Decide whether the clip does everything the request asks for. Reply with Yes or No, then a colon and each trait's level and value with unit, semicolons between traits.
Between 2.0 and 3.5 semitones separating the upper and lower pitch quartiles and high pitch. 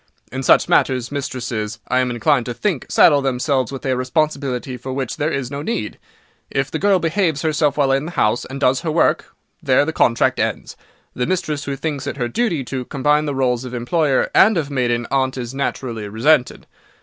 No: average, 3.2 semitones; low, 135 Hz